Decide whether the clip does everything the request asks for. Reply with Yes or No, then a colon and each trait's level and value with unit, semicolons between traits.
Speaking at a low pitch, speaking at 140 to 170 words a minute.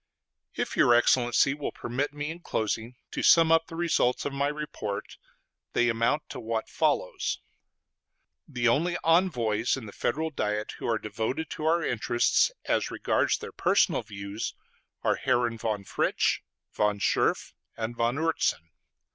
Yes: low, 120 Hz; average, 150 wpm